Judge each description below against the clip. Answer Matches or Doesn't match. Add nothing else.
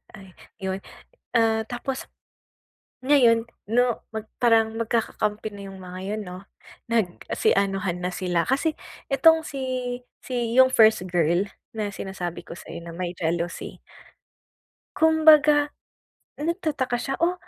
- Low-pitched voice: Doesn't match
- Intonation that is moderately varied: Doesn't match